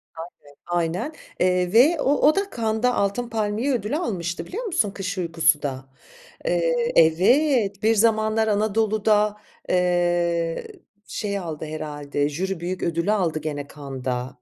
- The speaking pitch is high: Yes, high, 195 Hz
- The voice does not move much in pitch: No, average, 5.1 semitones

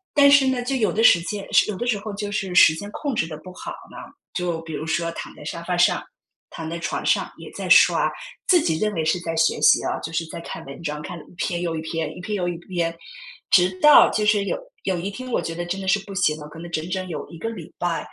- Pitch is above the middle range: No, medium, 175 Hz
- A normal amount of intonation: Yes, average, 4.0 semitones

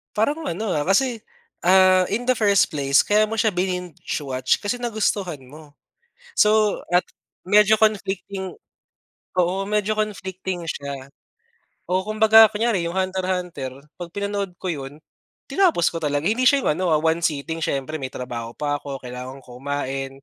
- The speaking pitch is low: No, medium, 185 Hz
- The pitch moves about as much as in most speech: No, wide, 6.5 semitones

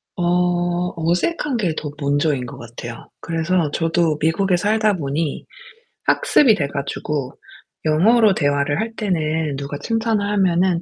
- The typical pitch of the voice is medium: Yes, medium, 170 Hz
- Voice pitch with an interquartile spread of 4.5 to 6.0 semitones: Yes, average, 5.1 semitones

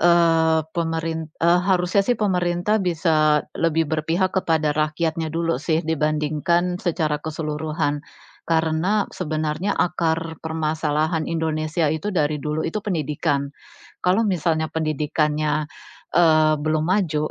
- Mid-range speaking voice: Yes, medium, 160 Hz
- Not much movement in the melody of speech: Yes, narrow, 2.0 semitones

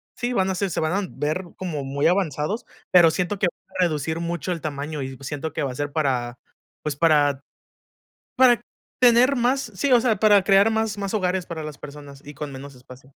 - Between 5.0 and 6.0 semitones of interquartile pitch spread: Yes, wide, 5.6 semitones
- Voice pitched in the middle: Yes, medium, 160 Hz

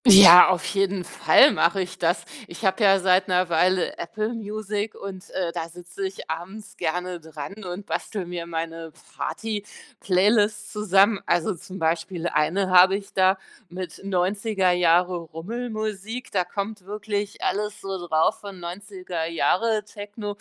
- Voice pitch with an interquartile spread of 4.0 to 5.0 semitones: No, average, 2.8 semitones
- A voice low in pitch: No, high, 190 Hz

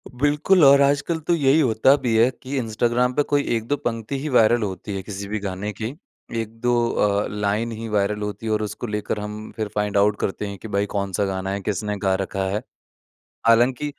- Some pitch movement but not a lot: Yes, average, 3.6 semitones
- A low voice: Yes, low, 110 Hz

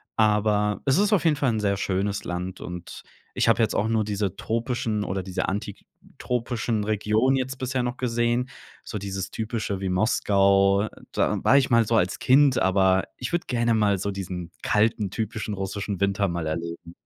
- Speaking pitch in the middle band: No, low, 105 Hz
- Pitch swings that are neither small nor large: Yes, average, 3.4 semitones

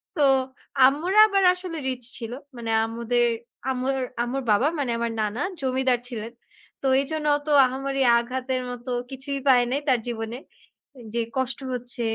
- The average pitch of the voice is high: Yes, very high, 255 Hz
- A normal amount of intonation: No, narrow, 2.2 semitones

